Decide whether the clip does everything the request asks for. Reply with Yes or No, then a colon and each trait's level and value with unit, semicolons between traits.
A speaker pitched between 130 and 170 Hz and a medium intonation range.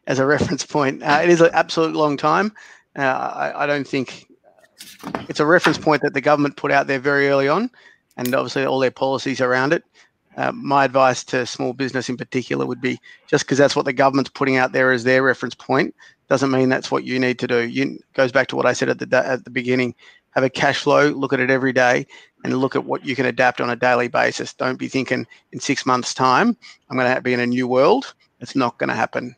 No: low, 135 Hz; narrow, 2.3 semitones